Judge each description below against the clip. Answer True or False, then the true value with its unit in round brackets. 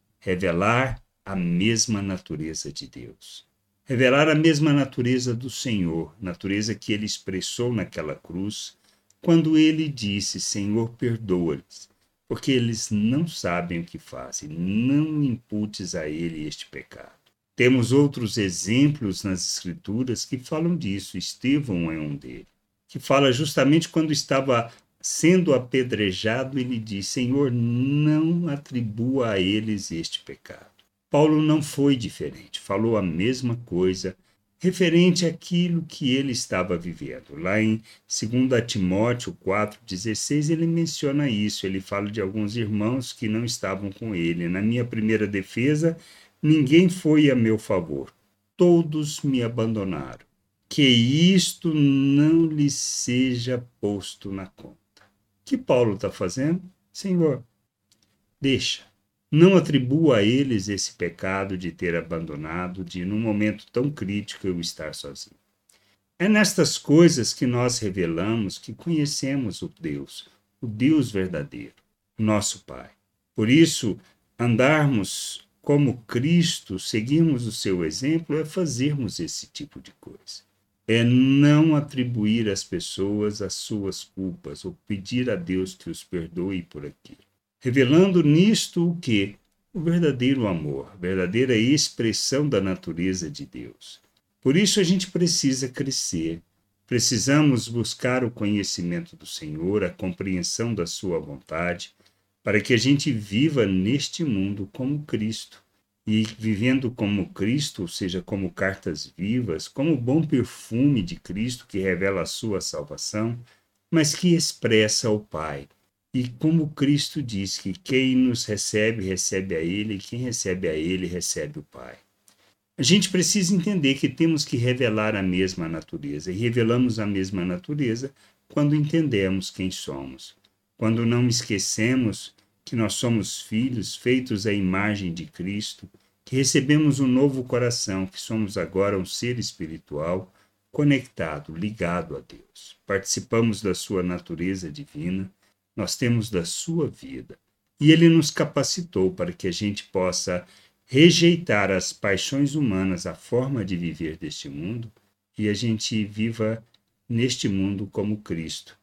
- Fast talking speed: False (135 wpm)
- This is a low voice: True (110 Hz)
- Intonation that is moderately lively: False (6.1 semitones)